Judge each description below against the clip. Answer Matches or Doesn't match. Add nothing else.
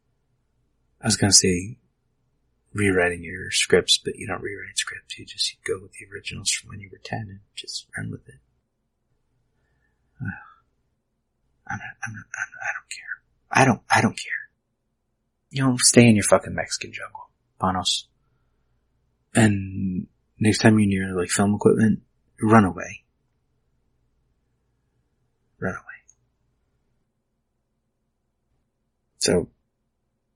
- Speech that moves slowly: Matches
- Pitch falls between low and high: Doesn't match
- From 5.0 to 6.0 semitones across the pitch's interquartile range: Doesn't match